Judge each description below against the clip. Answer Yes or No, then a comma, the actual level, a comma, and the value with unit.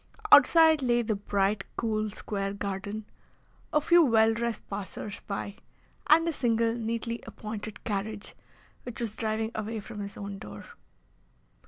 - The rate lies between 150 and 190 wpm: No, average, 140 wpm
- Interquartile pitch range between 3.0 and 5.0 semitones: No, narrow, 2.5 semitones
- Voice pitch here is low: No, high, 220 Hz